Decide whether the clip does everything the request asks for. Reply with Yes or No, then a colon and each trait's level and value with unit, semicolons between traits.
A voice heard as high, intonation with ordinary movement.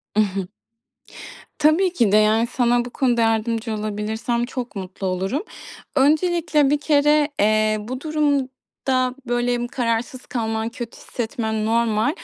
Yes: high, 240 Hz; average, 3.7 semitones